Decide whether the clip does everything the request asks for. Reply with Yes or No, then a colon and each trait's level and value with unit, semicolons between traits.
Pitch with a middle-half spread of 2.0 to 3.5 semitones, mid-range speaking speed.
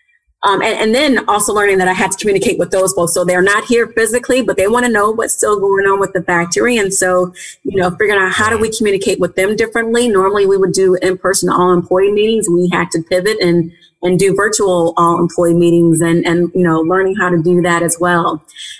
No: average, 3.1 semitones; fast, 230 wpm